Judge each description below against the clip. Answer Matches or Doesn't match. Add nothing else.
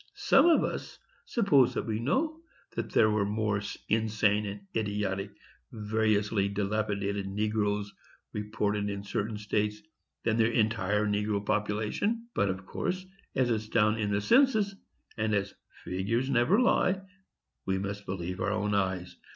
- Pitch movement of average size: Doesn't match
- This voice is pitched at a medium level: Doesn't match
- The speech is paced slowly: Doesn't match